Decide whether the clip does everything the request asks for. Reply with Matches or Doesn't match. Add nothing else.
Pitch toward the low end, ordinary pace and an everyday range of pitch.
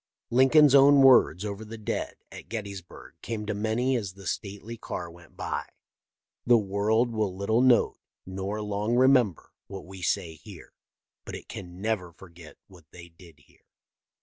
Matches